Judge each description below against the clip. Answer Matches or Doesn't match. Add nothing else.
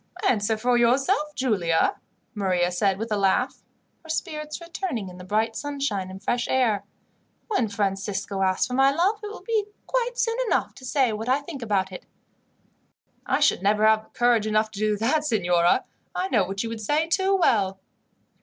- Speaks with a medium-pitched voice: Doesn't match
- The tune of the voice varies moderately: Doesn't match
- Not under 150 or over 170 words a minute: Doesn't match